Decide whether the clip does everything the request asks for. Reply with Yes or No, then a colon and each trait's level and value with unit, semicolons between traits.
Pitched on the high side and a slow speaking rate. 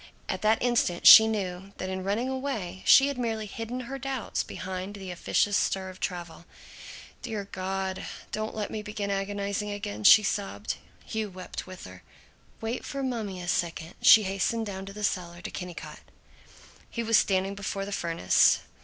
No: high, 200 Hz; average, 170 wpm